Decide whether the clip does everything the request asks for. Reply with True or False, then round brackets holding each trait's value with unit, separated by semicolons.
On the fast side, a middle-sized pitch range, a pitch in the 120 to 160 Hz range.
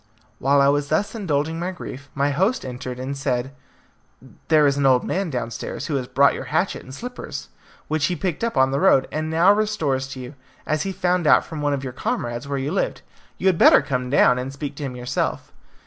True (225 wpm; 4.0 semitones; 140 Hz)